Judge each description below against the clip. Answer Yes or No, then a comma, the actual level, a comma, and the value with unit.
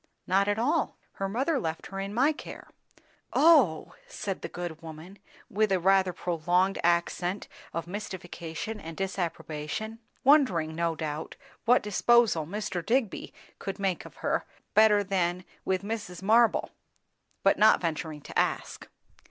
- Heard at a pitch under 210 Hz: Yes, high, 190 Hz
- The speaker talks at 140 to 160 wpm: Yes, average, 145 wpm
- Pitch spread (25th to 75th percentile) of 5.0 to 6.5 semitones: No, average, 4.2 semitones